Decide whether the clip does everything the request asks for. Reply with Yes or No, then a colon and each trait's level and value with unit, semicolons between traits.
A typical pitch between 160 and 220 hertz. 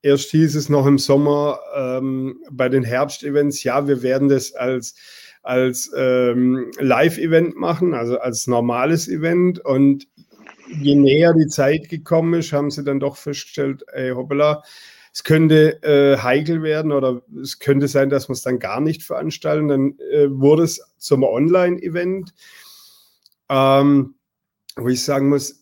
No: medium, 140 Hz